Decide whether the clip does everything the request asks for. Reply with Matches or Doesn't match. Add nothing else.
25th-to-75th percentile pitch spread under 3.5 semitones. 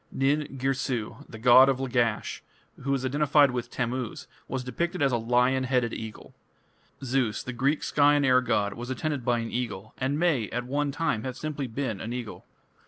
Matches